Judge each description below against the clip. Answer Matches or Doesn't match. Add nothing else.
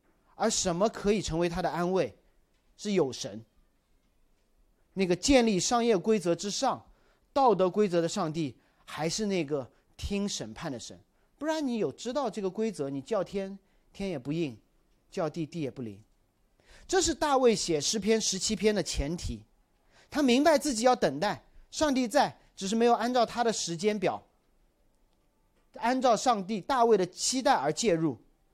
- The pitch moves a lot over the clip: Matches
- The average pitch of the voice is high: Matches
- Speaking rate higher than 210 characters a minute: Matches